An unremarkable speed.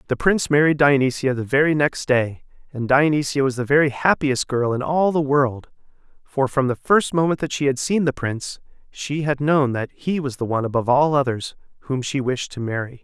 No: fast, 210 wpm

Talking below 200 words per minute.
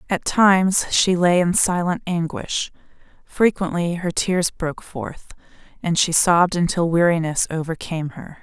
Yes: slow, 135 wpm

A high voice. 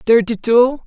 Yes: high, 235 Hz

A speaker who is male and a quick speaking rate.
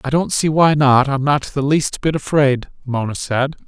Yes: male; fast, 210 wpm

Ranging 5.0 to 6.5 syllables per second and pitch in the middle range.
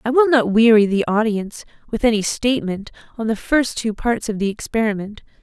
No: 5.6 syllables/s; high, 225 Hz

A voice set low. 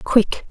No: high, 220 Hz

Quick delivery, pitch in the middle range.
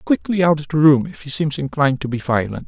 Yes: fast, 290 wpm; medium, 150 Hz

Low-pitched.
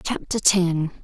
No: medium, 175 Hz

